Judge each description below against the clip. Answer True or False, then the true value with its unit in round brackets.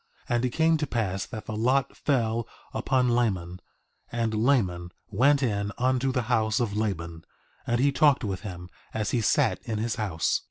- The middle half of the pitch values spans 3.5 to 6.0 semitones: True (3.9 semitones)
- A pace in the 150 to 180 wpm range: True (175 wpm)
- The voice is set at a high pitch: False (115 Hz)